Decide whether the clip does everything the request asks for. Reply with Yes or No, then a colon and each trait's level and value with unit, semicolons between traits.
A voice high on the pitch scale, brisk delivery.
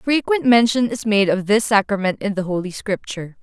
No: high, 210 Hz; average, 195 wpm